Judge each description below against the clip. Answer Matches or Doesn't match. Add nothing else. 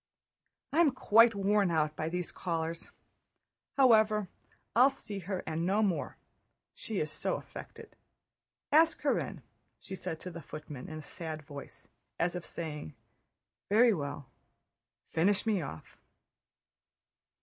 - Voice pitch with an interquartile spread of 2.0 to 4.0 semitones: Doesn't match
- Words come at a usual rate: Doesn't match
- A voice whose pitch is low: Doesn't match